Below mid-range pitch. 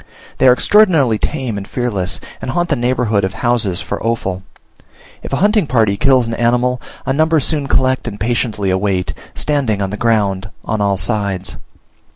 Yes: low, 120 Hz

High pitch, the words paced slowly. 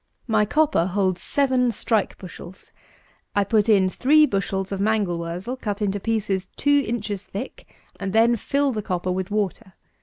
No: high, 205 Hz; average, 160 wpm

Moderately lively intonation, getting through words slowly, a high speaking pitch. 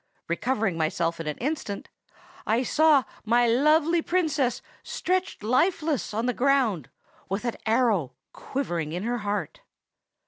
No: wide, 6.2 semitones; slow, 130 wpm; high, 240 Hz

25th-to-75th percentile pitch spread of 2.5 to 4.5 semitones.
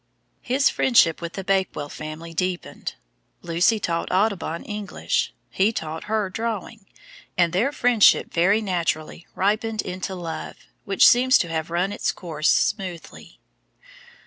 Yes: average, 4.2 semitones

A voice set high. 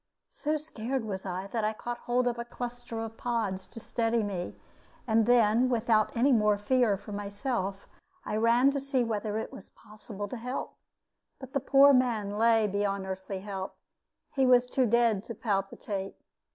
Yes: high, 225 Hz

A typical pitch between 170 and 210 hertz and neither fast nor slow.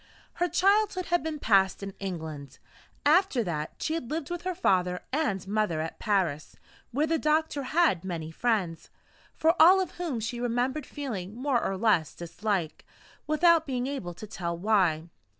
No: high, 230 Hz; average, 165 wpm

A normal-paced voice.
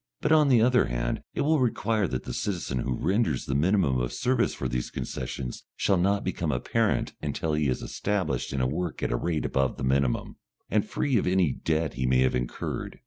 No: fast, 210 wpm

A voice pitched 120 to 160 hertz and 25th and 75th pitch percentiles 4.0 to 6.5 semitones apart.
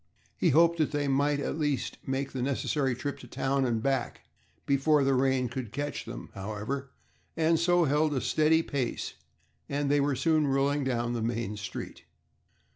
No: medium, 140 Hz; narrow, 2.5 semitones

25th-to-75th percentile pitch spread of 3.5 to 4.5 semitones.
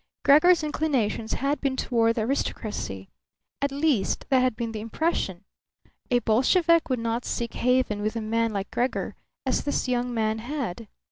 Yes: average, 4.0 semitones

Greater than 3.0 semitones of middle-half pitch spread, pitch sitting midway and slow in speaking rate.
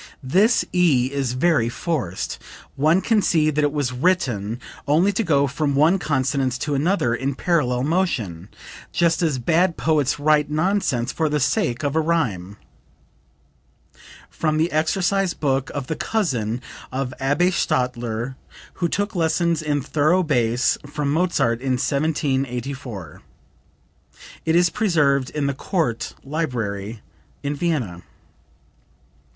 Yes: average, 4.8 semitones; medium, 145 Hz; slow, 130 wpm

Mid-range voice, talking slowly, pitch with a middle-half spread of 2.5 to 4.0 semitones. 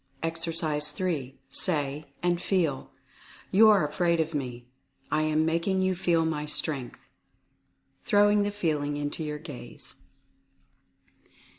Yes: medium, 160 Hz; slow, 125 wpm; average, 3.1 semitones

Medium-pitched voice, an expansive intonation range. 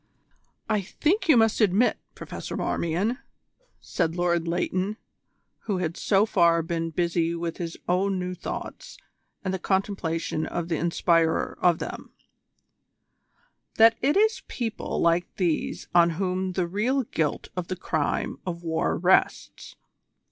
No: medium, 180 Hz; average, 3.5 semitones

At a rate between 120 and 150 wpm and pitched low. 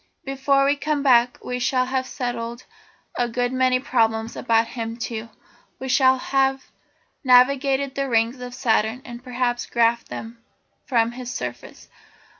No: average, 145 wpm; very high, 250 Hz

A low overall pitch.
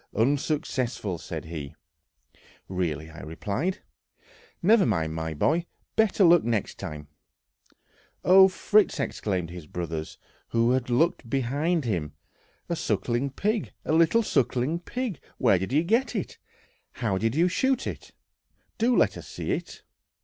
Yes: low, 125 Hz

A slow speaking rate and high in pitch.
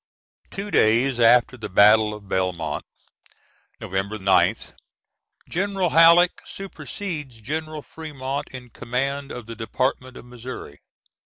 No: slow, 110 wpm; low, 125 Hz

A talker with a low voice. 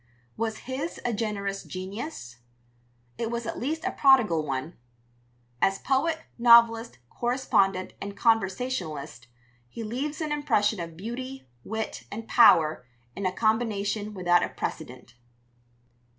No: high, 220 Hz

